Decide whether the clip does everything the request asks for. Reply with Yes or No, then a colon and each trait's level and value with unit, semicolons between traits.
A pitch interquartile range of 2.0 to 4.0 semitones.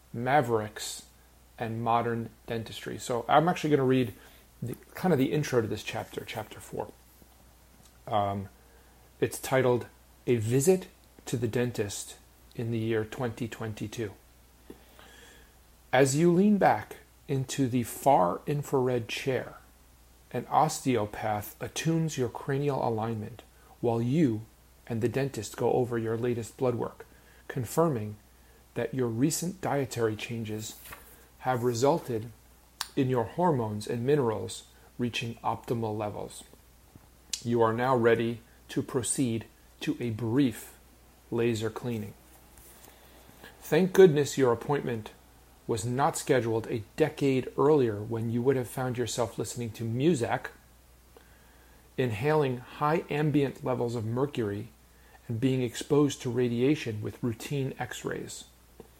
No: average, 4.7 semitones